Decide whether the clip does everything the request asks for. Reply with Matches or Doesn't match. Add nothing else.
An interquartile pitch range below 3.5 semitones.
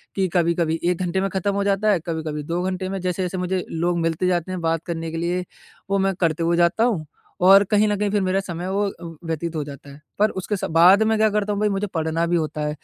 Matches